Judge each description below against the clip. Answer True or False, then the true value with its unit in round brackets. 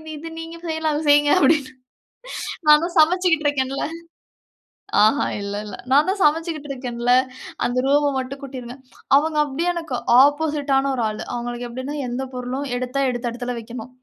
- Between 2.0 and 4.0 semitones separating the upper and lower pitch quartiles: True (3.6 semitones)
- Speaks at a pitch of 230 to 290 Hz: True (275 Hz)